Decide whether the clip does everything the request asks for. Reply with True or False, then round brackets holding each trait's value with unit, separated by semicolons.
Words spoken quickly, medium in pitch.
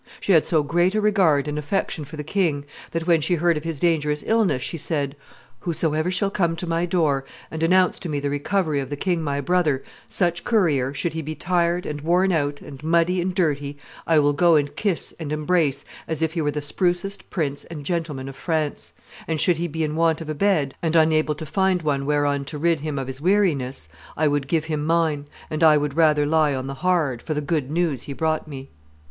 True (225 wpm; 155 Hz)